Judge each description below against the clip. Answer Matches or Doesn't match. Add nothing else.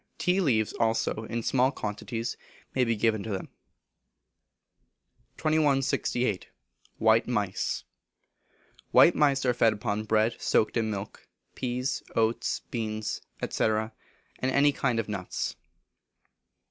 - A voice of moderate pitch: Doesn't match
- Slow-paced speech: Matches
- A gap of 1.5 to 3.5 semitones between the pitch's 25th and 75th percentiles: Matches